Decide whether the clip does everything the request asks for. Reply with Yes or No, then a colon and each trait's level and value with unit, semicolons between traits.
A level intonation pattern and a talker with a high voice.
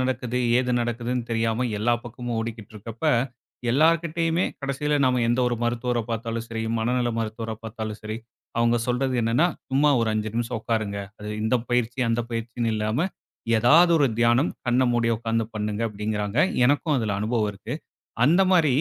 No: narrow, 2.2 semitones; low, 120 Hz